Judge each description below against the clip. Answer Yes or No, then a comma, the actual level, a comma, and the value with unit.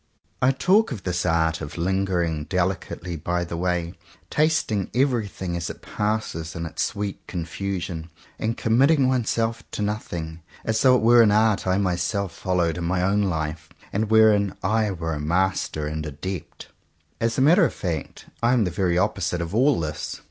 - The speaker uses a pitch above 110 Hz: No, very low, 95 Hz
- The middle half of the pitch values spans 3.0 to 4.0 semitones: No, average, 4.7 semitones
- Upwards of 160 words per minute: Yes, average, 175 wpm